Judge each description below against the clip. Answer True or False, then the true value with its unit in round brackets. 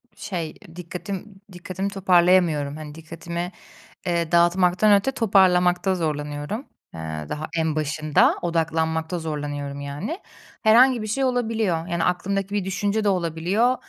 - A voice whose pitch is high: False (175 Hz)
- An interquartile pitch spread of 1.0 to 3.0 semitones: False (3.8 semitones)